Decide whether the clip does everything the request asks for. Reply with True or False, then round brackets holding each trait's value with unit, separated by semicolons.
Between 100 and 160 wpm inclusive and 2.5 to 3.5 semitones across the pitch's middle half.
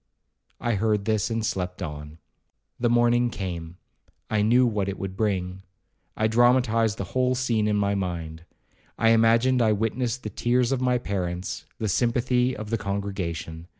False (155 wpm; 3.9 semitones)